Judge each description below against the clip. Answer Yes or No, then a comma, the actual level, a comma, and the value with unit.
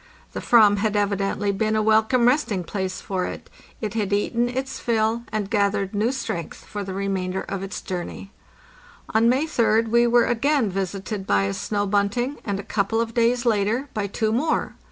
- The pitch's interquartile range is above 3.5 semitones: No, average, 3.0 semitones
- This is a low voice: No, high, 215 Hz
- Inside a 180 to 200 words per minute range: Yes, average, 185 wpm